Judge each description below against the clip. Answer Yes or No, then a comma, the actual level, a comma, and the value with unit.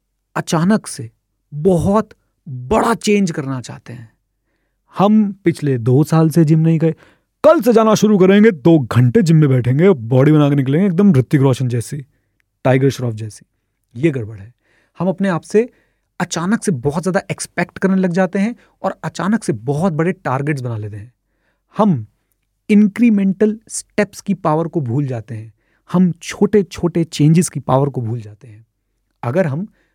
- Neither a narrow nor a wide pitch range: No, wide, 7.8 semitones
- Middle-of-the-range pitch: Yes, medium, 155 Hz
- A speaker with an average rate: Yes, average, 165 wpm